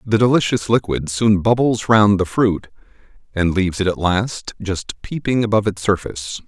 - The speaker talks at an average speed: Yes, average, 165 wpm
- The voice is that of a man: Yes, male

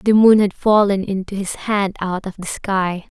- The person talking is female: Yes, female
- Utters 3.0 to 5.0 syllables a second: Yes, 4.4 syllables/s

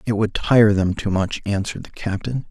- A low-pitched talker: Yes, low, 105 Hz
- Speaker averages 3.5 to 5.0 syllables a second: No, 5.2 syllables/s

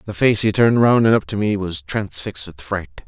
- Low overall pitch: Yes, low, 100 Hz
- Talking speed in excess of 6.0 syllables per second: No, 5.5 syllables/s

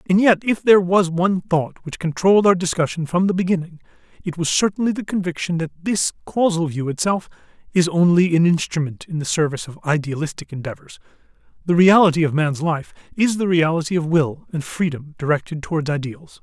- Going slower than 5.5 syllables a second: No, 5.8 syllables/s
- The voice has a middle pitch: Yes, medium, 170 Hz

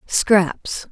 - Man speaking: No, female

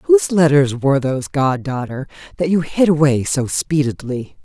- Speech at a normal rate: Yes, average, 160 wpm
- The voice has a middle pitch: Yes, medium, 145 Hz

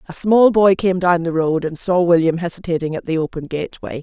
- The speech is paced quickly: Yes, fast, 225 wpm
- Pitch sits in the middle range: Yes, medium, 170 Hz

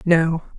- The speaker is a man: No, female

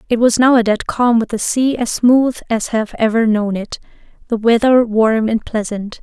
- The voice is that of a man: No, female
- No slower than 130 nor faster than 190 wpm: No, average, 200 wpm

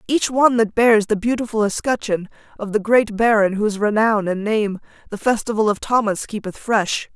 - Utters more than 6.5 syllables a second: No, 5.2 syllables/s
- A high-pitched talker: Yes, high, 215 Hz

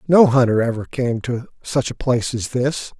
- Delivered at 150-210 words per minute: Yes, average, 200 wpm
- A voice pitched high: No, low, 125 Hz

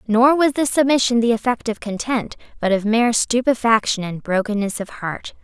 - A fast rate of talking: No, average, 175 wpm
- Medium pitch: No, high, 230 Hz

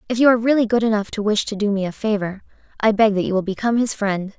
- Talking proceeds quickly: Yes, fast, 290 wpm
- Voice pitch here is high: Yes, high, 210 Hz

